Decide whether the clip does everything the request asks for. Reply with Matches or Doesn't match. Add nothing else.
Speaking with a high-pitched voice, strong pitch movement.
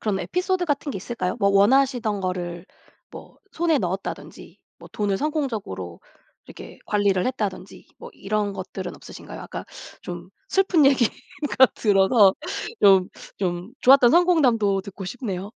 Matches